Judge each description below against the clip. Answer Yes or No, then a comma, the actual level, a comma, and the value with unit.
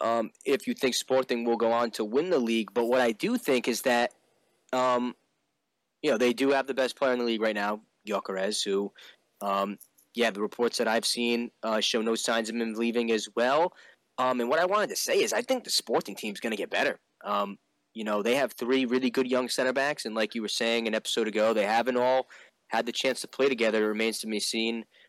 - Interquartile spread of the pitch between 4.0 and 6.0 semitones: No, narrow, 2.4 semitones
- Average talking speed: No, fast, 240 wpm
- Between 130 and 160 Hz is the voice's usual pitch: No, low, 115 Hz